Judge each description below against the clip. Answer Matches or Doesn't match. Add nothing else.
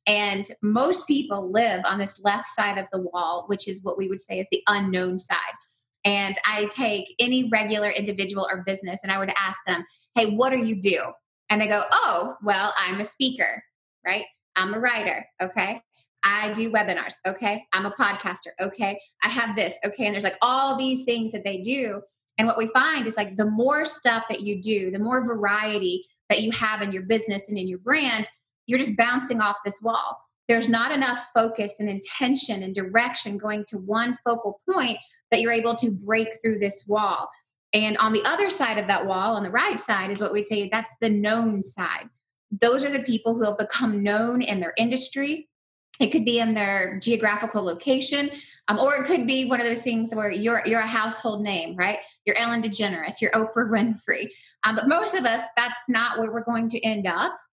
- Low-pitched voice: Doesn't match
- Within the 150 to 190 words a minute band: Doesn't match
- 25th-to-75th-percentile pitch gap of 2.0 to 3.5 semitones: Matches